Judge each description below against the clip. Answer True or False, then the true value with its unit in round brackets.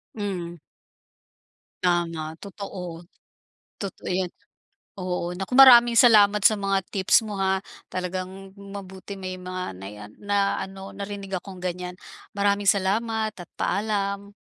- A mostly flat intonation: True (1.8 semitones)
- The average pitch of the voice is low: False (195 Hz)